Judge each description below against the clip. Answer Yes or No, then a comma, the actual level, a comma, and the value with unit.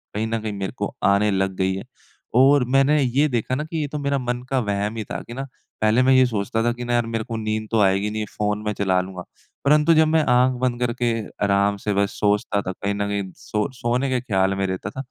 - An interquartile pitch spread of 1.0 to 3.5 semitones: No, average, 4.2 semitones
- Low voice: Yes, low, 110 Hz